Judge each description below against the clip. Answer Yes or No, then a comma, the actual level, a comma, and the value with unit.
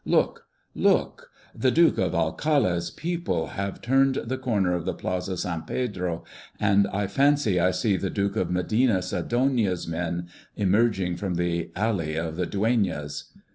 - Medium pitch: No, very low, 95 Hz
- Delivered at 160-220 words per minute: No, average, 150 wpm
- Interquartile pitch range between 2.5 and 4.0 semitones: No, average, 5.1 semitones